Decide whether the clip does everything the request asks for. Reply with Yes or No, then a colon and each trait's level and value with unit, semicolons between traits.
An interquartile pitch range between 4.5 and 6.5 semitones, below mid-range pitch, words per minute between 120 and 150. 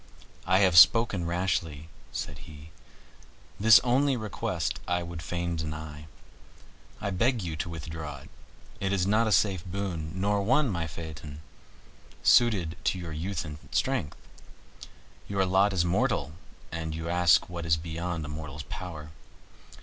No: average, 3.8 semitones; very low, 85 Hz; average, 145 wpm